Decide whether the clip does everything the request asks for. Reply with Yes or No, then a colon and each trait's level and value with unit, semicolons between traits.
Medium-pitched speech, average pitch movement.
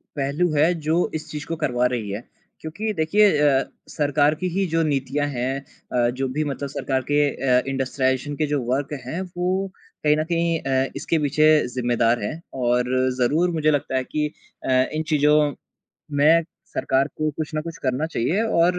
Yes: medium, 145 Hz; average, 3.2 semitones